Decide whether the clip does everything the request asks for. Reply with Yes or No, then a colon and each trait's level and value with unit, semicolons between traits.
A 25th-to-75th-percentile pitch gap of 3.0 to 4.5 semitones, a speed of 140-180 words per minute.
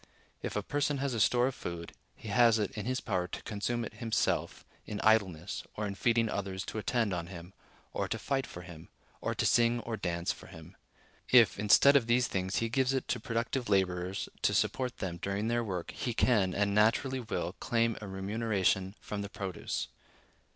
No: average, 3.8 semitones; average, 200 wpm